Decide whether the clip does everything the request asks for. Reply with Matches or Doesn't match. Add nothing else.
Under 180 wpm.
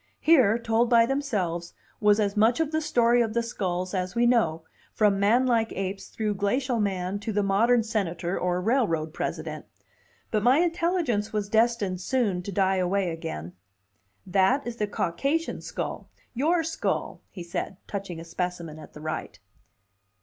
Matches